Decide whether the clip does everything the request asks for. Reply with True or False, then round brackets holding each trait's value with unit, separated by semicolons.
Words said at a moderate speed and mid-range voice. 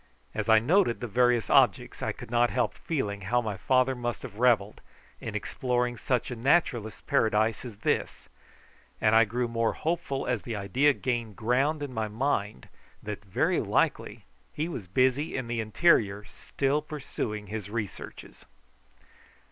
False (155 wpm; 120 Hz)